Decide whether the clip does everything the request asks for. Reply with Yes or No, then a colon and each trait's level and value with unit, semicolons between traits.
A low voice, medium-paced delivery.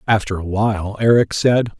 Yes: low, 105 Hz; average, 165 wpm